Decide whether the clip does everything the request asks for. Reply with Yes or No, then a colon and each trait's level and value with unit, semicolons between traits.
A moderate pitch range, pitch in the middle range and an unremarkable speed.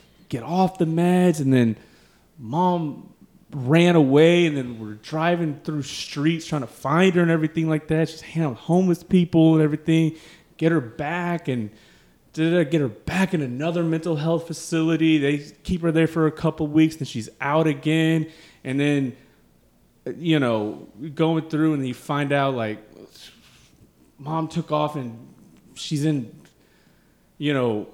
Yes: average, 3.2 semitones; medium, 155 Hz; average, 160 wpm